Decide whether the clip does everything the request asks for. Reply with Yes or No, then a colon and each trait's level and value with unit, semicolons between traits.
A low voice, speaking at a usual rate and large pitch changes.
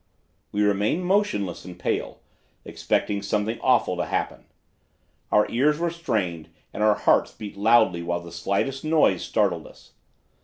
Yes: low, 105 Hz; average, 145 wpm; wide, 6.3 semitones